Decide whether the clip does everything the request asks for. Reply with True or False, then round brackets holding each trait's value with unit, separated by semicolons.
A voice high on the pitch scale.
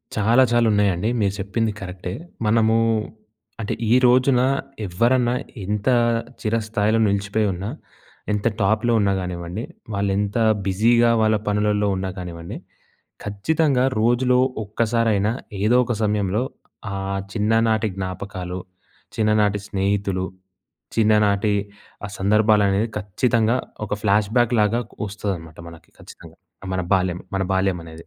False (105 Hz)